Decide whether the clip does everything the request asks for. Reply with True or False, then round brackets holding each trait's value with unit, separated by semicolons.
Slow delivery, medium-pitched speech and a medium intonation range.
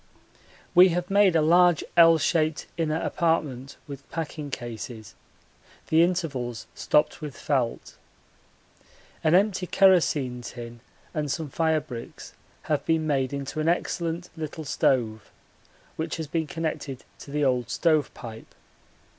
True (130 wpm; 155 Hz; 3.8 semitones)